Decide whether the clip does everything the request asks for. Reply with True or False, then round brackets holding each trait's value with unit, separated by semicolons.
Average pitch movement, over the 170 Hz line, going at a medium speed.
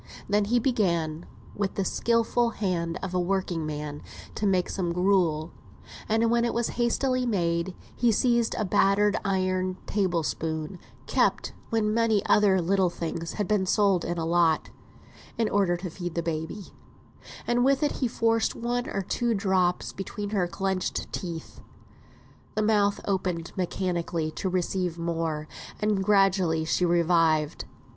True (3.7 semitones; 190 Hz; 150 wpm)